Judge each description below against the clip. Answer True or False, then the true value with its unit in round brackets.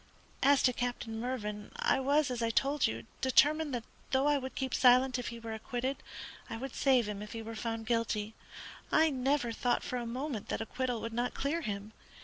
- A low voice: False (245 Hz)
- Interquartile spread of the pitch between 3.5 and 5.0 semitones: False (2.9 semitones)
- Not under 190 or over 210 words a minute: True (205 wpm)